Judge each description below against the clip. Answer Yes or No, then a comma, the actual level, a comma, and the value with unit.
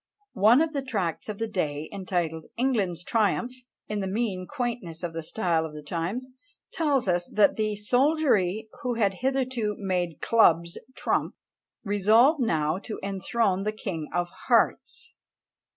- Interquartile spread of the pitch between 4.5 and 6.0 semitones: Yes, average, 5.2 semitones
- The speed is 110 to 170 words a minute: Yes, average, 150 wpm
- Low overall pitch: No, high, 205 Hz